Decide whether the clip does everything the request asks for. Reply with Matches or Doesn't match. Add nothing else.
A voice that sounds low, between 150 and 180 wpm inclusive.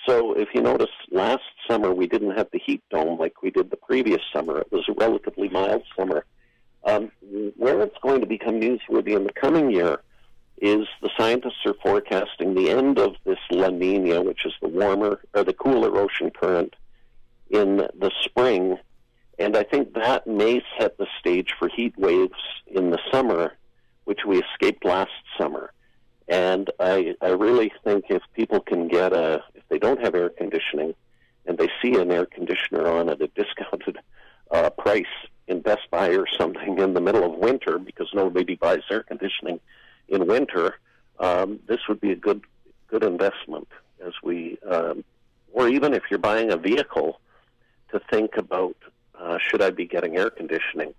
Matches